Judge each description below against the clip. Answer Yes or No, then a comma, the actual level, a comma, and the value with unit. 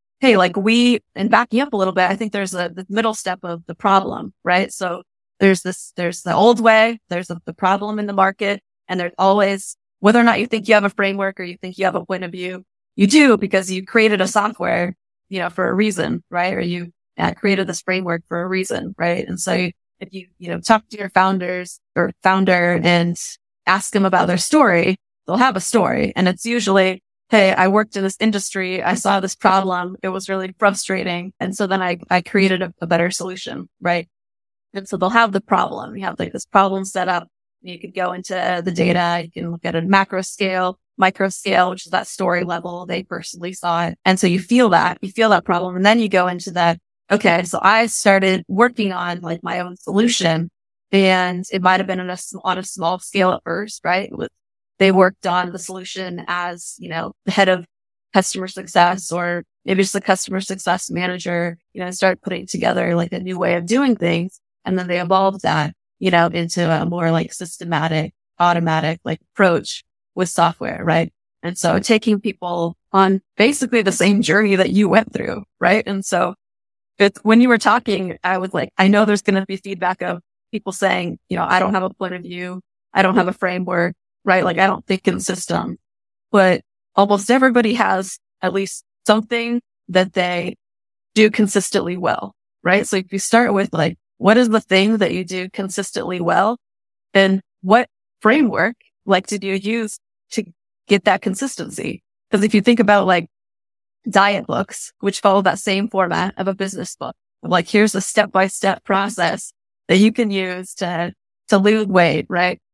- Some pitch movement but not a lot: No, narrow, 2.3 semitones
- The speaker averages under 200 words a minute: No, fast, 205 wpm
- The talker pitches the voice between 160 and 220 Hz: Yes, high, 190 Hz